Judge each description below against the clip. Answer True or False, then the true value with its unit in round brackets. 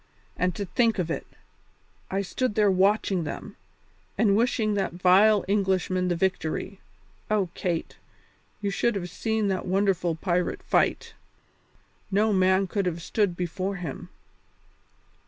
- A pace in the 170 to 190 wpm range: False (135 wpm)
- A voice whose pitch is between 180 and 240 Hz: True (190 Hz)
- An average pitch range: False (2.3 semitones)